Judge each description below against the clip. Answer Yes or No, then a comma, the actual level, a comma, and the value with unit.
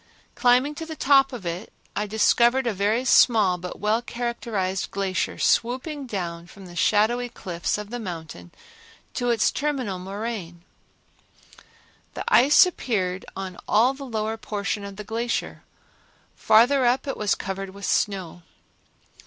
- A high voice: Yes, high, 215 Hz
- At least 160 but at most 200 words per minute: No, average, 145 wpm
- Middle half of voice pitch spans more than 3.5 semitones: Yes, average, 4.3 semitones